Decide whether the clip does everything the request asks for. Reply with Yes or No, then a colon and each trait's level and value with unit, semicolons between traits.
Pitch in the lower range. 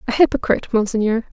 No: high, 230 Hz